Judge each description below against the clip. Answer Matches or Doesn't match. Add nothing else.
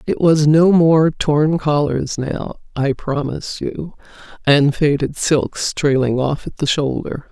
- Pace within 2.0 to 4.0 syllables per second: Matches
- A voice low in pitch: Doesn't match